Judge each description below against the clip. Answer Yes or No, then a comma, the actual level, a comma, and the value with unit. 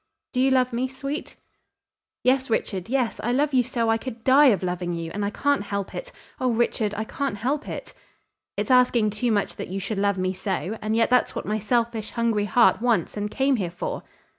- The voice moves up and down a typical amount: Yes, average, 4.0 semitones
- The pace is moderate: No, fast, 215 wpm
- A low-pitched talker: No, high, 230 Hz